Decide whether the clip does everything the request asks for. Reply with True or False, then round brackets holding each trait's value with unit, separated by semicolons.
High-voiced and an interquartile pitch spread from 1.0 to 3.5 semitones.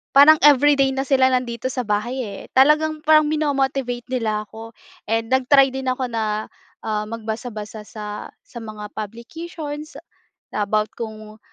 False (245 Hz; 4.1 semitones)